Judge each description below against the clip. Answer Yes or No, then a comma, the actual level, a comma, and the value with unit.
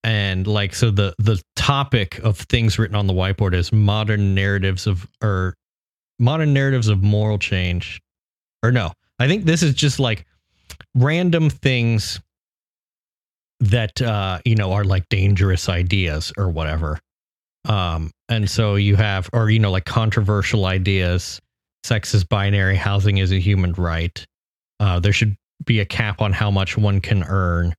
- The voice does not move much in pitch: No, average, 3.2 semitones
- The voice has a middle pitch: No, low, 100 Hz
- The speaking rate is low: No, average, 160 wpm